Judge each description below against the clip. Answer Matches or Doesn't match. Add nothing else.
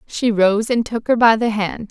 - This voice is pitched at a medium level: Doesn't match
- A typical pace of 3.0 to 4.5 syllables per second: Matches